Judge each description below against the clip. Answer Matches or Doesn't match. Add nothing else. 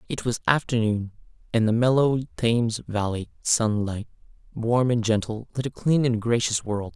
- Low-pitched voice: Matches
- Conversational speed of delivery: Matches